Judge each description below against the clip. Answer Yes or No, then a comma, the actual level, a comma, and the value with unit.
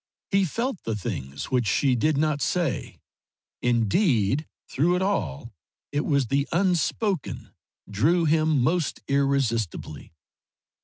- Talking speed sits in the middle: No, slow, 115 wpm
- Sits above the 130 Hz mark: Yes, medium, 140 Hz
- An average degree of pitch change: No, wide, 6.4 semitones